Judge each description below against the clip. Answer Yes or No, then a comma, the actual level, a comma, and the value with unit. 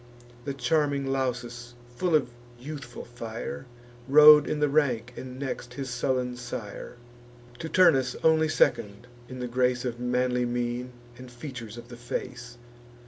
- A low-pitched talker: Yes, low, 125 Hz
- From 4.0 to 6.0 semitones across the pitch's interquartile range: No, narrow, 2.4 semitones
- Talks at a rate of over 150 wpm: No, average, 140 wpm